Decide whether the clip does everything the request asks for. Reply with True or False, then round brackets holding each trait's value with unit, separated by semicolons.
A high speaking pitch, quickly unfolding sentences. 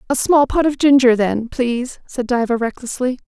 False (250 Hz; 185 wpm)